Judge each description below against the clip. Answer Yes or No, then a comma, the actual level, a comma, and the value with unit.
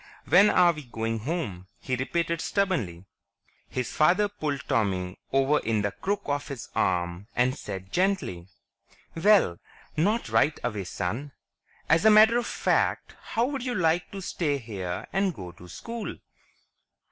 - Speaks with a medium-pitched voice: Yes, medium, 145 Hz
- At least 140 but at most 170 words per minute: Yes, average, 150 wpm